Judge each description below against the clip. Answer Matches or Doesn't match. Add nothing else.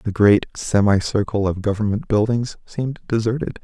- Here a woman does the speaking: Doesn't match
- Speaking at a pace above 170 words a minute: Doesn't match